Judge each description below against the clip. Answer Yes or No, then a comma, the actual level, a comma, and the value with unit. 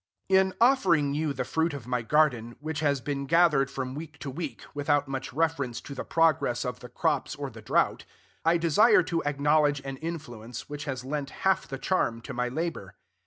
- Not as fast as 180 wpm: No, average, 195 wpm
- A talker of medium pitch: Yes, medium, 145 Hz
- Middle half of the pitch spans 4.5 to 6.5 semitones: No, average, 3.7 semitones